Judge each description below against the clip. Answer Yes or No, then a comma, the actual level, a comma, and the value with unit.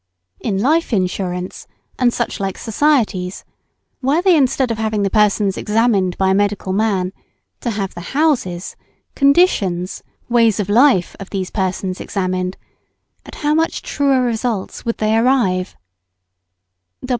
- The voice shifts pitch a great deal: No, average, 5.0 semitones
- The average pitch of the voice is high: Yes, high, 210 Hz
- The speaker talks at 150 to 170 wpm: No, slow, 135 wpm